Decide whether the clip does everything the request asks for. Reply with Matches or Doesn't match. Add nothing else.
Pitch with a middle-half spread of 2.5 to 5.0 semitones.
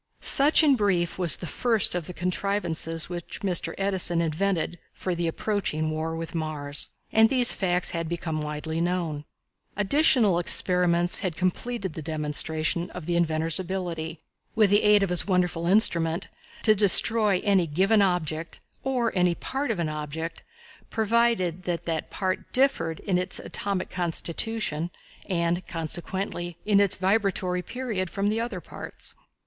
Matches